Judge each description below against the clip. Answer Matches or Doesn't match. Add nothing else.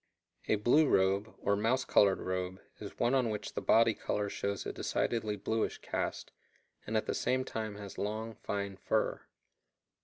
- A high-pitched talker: Doesn't match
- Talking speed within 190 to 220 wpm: Doesn't match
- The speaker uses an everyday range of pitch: Doesn't match